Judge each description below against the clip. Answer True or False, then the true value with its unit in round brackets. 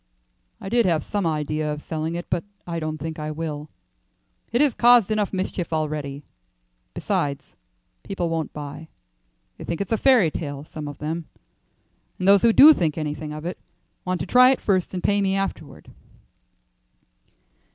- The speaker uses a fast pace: False (170 wpm)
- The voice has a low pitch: False (165 Hz)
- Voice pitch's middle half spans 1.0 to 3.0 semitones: False (4.4 semitones)